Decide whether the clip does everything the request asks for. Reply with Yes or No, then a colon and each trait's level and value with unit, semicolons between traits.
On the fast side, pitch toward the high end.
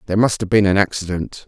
No: fast, 245 wpm; low, 100 Hz